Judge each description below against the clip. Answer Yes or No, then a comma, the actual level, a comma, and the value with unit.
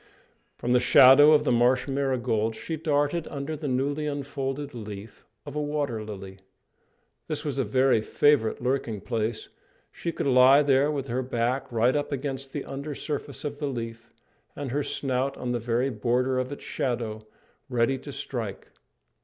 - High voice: No, low, 130 Hz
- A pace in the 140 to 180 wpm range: Yes, average, 170 wpm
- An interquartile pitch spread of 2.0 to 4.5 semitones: Yes, average, 3.2 semitones